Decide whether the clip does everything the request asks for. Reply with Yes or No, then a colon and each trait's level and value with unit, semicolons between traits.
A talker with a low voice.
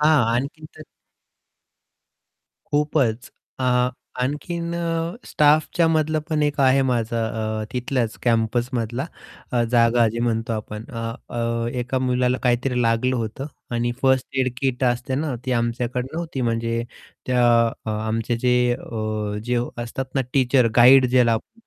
Yes: low, 125 Hz